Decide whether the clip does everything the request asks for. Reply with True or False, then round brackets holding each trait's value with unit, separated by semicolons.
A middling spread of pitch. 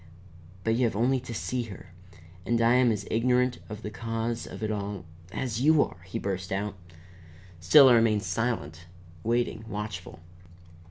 True (3.1 semitones)